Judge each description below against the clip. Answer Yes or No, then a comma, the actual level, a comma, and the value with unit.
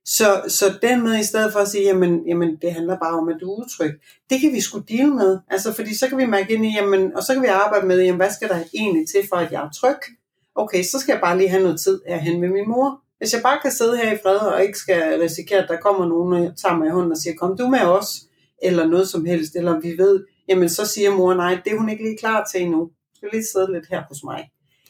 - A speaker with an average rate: No, fast, 290 wpm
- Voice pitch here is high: Yes, high, 195 Hz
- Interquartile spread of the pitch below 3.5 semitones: No, average, 3.9 semitones